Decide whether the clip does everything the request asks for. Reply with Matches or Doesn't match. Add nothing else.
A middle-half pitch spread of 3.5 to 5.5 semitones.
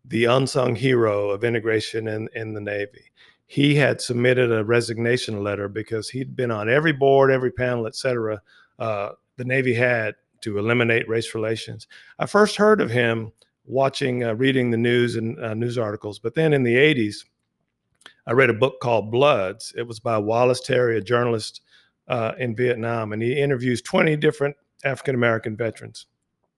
Doesn't match